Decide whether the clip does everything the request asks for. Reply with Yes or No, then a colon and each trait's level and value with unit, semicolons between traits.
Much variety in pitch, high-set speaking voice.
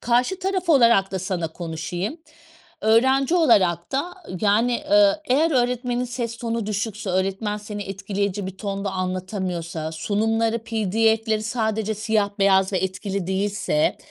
No: average, 3.8 semitones; high, 215 Hz